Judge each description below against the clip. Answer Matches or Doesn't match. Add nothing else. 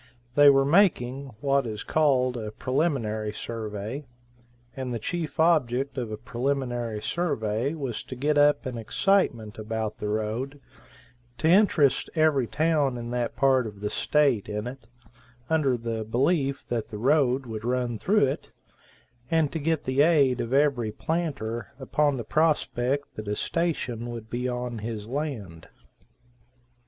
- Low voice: Matches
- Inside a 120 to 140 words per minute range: Doesn't match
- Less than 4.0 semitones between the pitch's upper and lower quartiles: Doesn't match